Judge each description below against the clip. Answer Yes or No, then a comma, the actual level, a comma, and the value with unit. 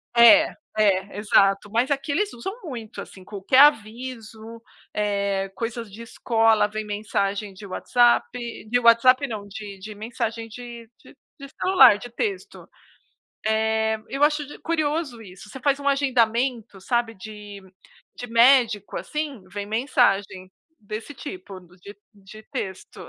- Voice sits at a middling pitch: No, high, 225 Hz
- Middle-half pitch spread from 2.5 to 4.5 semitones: Yes, average, 3.9 semitones